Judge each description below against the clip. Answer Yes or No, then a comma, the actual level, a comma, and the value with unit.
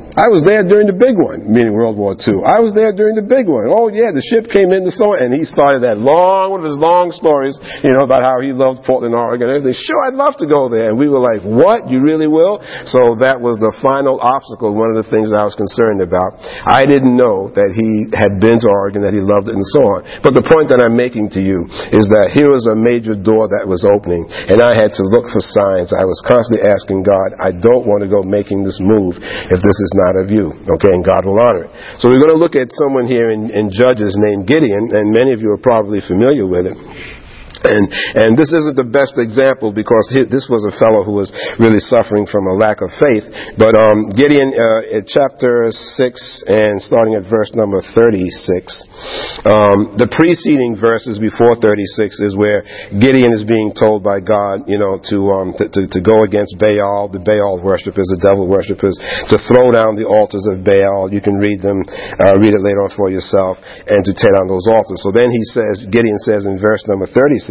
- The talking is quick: Yes, fast, 235 wpm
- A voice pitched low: Yes, low, 110 Hz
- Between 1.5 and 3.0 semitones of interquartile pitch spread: No, average, 4.1 semitones